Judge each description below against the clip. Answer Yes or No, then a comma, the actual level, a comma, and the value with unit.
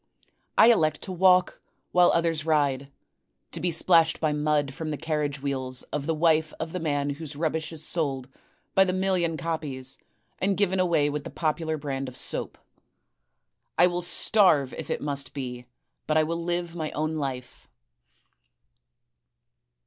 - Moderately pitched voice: Yes, medium, 155 Hz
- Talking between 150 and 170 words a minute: Yes, average, 160 wpm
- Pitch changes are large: No, average, 3.1 semitones